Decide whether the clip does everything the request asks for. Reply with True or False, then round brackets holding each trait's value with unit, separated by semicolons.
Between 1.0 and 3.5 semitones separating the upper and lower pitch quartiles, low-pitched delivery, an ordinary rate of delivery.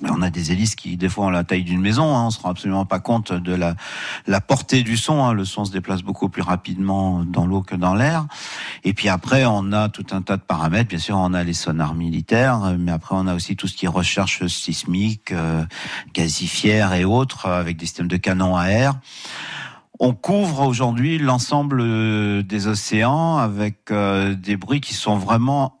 False (4.2 semitones; 100 Hz; 210 wpm)